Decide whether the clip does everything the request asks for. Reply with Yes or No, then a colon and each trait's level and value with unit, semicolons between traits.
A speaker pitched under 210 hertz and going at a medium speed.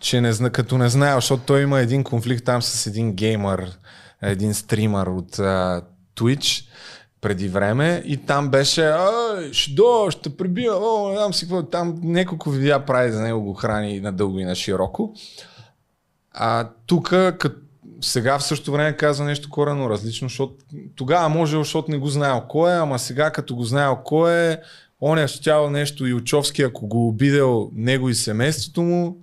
No: low, 135 Hz; fast, 175 wpm